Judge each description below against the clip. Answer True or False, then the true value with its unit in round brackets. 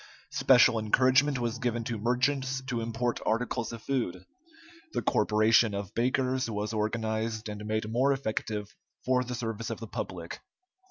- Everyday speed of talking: True (150 wpm)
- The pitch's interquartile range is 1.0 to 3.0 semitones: True (2.7 semitones)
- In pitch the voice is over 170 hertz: False (115 Hz)